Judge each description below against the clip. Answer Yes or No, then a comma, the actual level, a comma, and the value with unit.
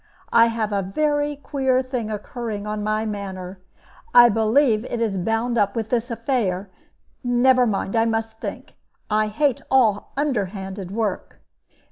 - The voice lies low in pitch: No, high, 225 Hz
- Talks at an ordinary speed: Yes, average, 145 wpm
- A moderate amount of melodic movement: Yes, average, 3.0 semitones